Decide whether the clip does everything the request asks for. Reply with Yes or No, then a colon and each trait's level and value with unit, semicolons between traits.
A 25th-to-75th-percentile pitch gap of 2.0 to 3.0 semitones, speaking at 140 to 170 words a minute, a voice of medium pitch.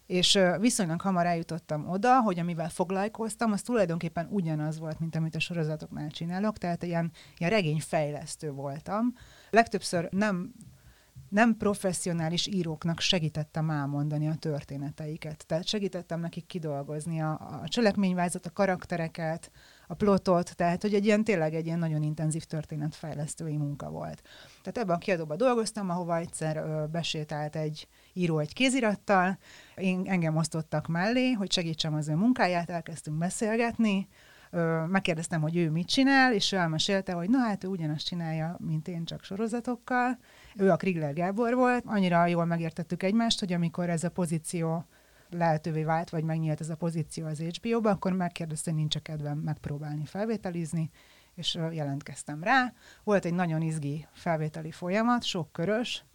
No: average, 3.7 semitones; average, 145 wpm; medium, 170 Hz